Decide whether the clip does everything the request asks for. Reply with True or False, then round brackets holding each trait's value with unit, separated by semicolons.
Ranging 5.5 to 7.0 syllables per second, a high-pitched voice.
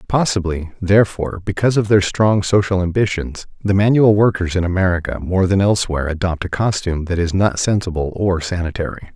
False (5.9 syllables/s; 95 Hz)